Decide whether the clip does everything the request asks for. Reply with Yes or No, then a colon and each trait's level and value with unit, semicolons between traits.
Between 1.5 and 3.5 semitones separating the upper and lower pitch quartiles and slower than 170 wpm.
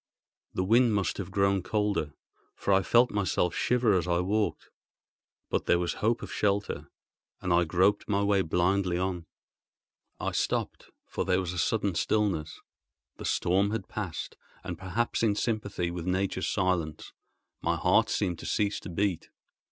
Yes: average, 2.7 semitones; average, 160 wpm